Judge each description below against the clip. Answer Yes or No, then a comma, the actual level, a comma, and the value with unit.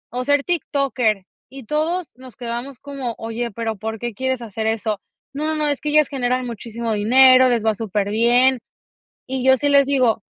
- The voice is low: No, very high, 250 Hz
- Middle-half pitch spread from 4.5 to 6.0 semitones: No, average, 3.6 semitones